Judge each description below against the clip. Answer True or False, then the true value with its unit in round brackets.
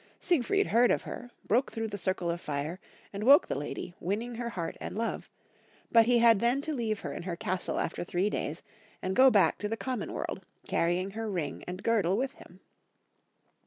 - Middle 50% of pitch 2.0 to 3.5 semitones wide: False (4.8 semitones)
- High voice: True (210 Hz)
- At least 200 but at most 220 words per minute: True (205 wpm)